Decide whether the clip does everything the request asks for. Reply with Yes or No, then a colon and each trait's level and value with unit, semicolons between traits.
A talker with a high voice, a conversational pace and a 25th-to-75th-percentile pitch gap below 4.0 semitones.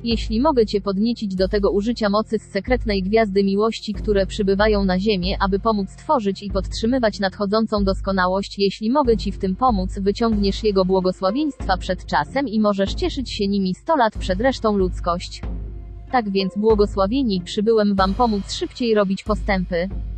Yes: high, 205 Hz; average, 160 wpm; narrow, 2.6 semitones